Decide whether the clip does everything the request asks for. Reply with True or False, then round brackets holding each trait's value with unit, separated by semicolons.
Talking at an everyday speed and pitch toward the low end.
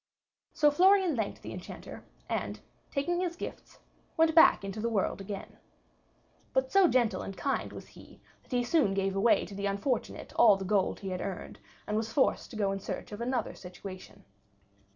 False (185 wpm; 220 Hz)